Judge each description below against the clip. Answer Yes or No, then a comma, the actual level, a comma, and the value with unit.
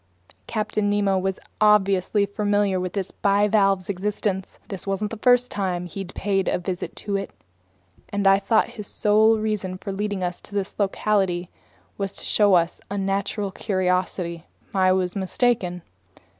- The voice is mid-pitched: No, high, 195 Hz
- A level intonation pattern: Yes, narrow, 1.9 semitones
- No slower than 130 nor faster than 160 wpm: Yes, average, 150 wpm